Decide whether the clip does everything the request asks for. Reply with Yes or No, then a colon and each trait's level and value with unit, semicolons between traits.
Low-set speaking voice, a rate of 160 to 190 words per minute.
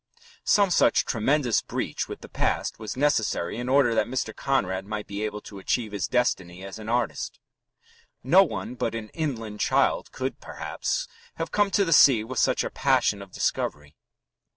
Yes: low, 115 Hz; average, 175 wpm